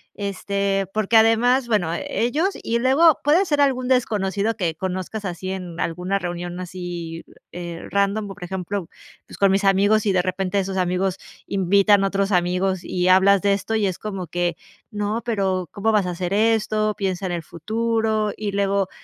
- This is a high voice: Yes, high, 195 Hz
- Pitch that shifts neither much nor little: Yes, average, 3.0 semitones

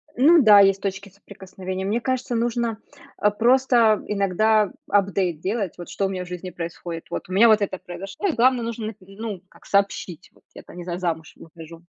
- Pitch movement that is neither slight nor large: Yes, average, 3.7 semitones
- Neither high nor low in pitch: No, high, 200 Hz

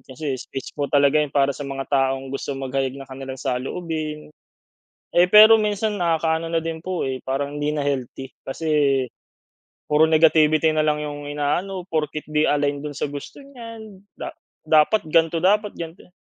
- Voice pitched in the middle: Yes, medium, 150 Hz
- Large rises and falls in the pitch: No, average, 3.1 semitones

